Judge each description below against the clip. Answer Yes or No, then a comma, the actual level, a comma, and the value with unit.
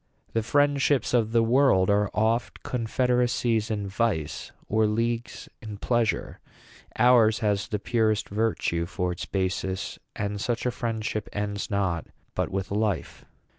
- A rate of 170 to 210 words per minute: No, slow, 135 wpm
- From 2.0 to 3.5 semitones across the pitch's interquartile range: Yes, average, 2.7 semitones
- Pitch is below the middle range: Yes, low, 110 Hz